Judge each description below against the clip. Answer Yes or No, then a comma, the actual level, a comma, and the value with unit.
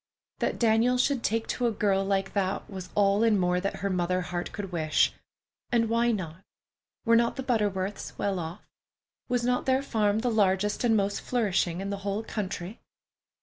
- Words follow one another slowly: No, average, 185 wpm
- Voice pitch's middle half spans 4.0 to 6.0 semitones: No, average, 3.4 semitones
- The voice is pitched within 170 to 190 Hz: No, high, 205 Hz